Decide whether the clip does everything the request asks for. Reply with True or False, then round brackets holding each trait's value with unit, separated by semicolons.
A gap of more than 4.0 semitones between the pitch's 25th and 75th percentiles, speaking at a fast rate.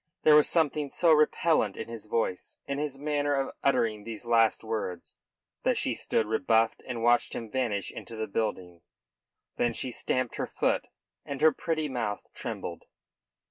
False (4.6 semitones; 165 wpm)